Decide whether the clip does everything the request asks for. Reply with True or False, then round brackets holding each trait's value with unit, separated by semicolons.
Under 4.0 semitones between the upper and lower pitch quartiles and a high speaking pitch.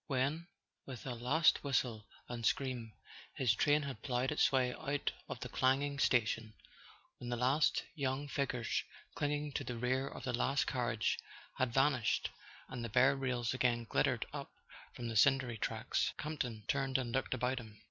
False (2.6 semitones; 130 Hz)